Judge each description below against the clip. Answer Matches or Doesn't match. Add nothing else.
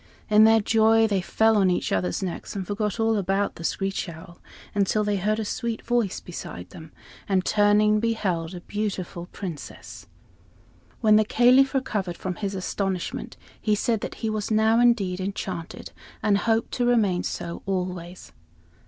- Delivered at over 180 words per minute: Doesn't match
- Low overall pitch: Doesn't match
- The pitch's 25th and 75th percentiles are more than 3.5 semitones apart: Doesn't match